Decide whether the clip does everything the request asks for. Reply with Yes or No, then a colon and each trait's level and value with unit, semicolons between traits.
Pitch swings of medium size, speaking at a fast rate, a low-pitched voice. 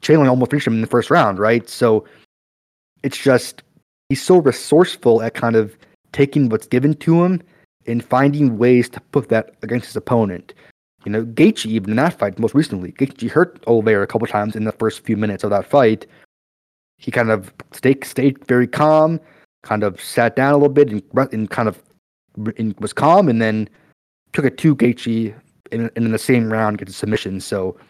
No: average, 4.1 semitones; average, 195 wpm; low, 115 Hz